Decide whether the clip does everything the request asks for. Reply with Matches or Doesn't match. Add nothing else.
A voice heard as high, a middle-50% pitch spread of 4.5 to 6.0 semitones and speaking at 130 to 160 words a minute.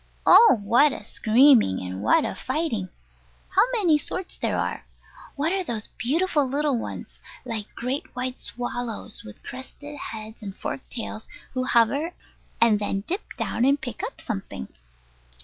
Matches